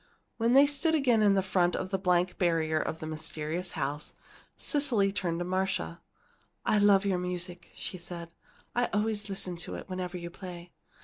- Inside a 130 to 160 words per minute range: No, average, 175 wpm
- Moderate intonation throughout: Yes, average, 3.0 semitones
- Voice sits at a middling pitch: Yes, medium, 180 Hz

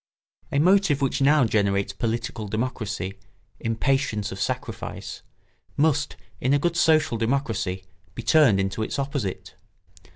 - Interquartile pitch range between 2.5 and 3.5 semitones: No, wide, 5.6 semitones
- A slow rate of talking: Yes, slow, 125 wpm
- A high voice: No, low, 120 Hz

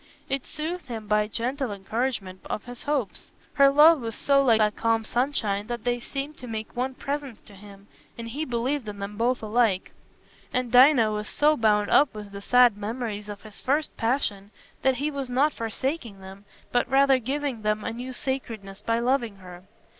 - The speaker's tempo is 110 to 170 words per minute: No, average, 190 wpm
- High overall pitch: Yes, high, 235 Hz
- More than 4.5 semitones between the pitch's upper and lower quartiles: No, average, 4.2 semitones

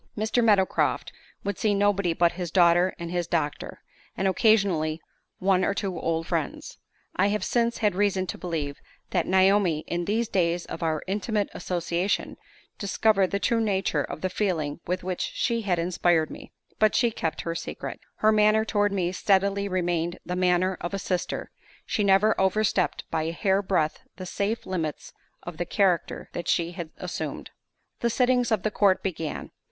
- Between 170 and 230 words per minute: Yes, average, 175 wpm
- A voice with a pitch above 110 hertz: Yes, medium, 185 Hz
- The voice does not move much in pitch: No, average, 3.0 semitones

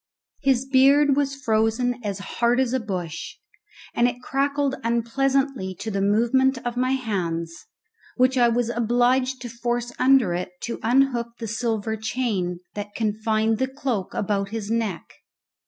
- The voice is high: Yes, high, 235 Hz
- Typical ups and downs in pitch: Yes, average, 3.4 semitones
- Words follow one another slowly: No, average, 150 wpm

